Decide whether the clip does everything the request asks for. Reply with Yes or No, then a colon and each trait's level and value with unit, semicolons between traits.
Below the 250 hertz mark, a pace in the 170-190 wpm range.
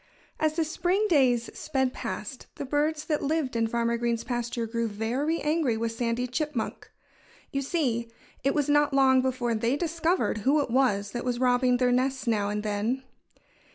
No: very high, 255 Hz; average, 175 wpm